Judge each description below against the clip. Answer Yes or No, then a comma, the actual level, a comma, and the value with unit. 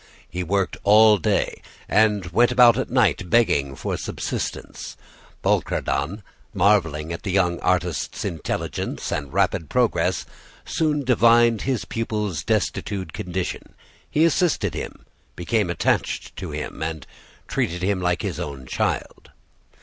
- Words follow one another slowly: Yes, slow, 125 wpm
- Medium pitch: No, very low, 95 Hz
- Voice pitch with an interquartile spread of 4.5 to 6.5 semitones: Yes, average, 5.0 semitones